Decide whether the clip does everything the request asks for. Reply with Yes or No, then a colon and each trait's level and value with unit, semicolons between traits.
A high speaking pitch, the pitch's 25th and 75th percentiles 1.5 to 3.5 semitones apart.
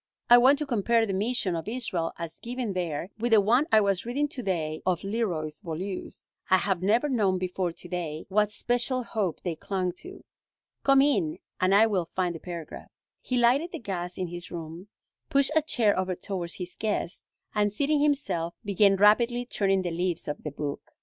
No: high, 195 Hz; average, 5.3 semitones